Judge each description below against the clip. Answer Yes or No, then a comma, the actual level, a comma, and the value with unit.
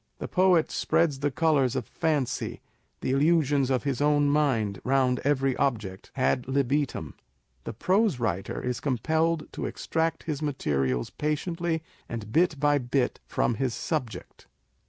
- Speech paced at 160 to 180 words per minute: No, average, 140 wpm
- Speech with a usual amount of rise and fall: Yes, average, 3.9 semitones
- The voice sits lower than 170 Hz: Yes, medium, 140 Hz